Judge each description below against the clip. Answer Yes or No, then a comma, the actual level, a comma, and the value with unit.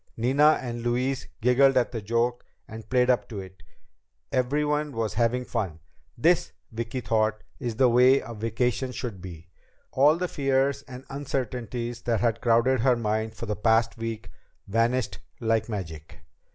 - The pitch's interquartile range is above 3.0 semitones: No, narrow, 2.5 semitones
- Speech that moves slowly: No, average, 155 wpm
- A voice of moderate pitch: No, low, 120 Hz